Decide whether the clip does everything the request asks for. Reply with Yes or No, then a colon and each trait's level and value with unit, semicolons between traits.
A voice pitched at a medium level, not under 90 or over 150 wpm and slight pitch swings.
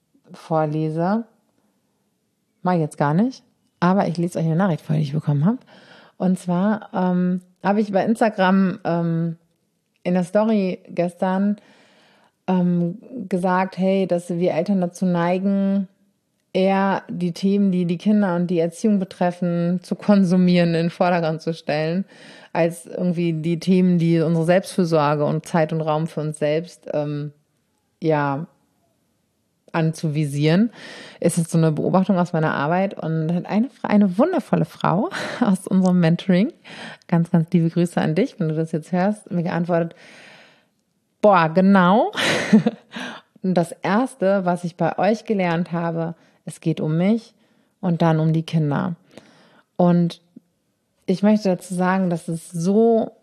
No: medium, 180 Hz; average, 145 wpm; average, 3.2 semitones